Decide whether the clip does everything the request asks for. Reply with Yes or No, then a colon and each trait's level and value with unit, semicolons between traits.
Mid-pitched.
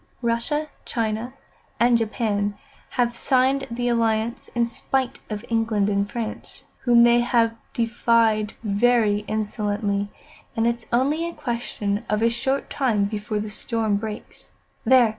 No: high, 230 Hz